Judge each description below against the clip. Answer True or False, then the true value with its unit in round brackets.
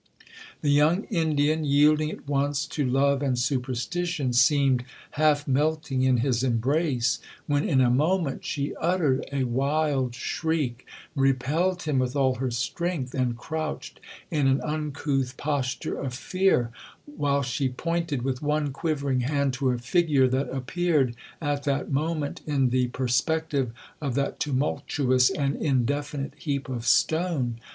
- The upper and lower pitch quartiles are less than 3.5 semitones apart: True (2.9 semitones)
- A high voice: False (140 Hz)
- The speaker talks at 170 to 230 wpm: False (140 wpm)